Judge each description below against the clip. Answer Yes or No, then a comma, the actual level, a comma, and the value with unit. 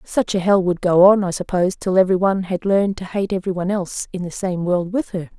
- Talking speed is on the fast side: Yes, fast, 265 wpm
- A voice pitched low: No, medium, 185 Hz